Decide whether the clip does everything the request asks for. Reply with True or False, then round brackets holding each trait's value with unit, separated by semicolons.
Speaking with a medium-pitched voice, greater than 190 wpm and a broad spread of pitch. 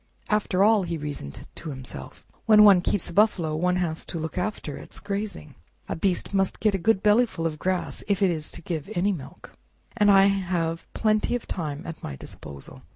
False (180 Hz; 200 wpm; 4.3 semitones)